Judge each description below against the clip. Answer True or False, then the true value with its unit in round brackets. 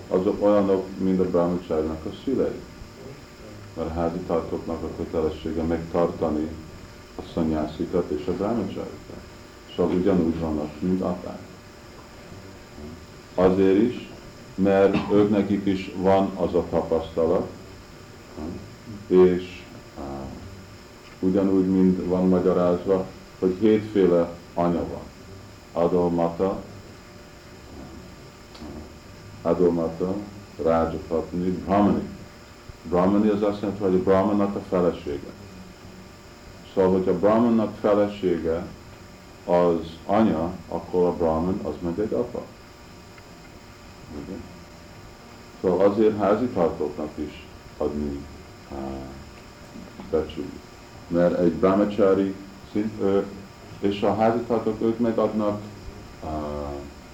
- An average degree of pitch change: True (3.4 semitones)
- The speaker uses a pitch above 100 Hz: False (95 Hz)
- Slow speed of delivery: True (95 wpm)